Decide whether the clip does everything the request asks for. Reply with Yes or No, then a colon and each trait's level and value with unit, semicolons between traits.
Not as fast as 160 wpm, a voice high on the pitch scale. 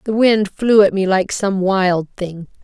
No: fast, 205 wpm; high, 195 Hz